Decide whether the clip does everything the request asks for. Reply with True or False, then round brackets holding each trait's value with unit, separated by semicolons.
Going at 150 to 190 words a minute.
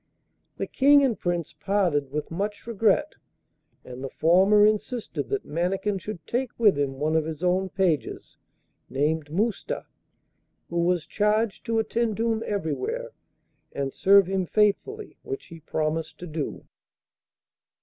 False (140 wpm)